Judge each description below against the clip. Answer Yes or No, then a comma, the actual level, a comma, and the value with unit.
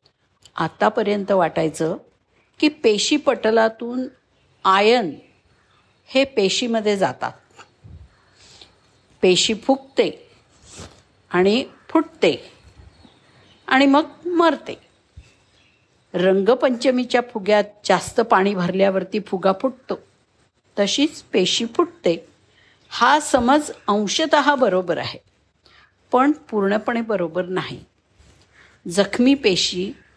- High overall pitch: Yes, high, 210 Hz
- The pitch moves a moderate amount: No, wide, 6.7 semitones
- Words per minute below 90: Yes, slow, 80 wpm